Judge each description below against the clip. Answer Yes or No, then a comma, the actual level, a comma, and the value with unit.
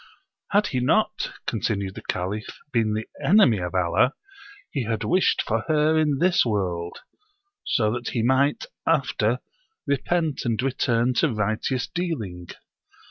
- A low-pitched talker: Yes, low, 120 Hz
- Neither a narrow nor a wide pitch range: No, wide, 5.9 semitones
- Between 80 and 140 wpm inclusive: Yes, slow, 135 wpm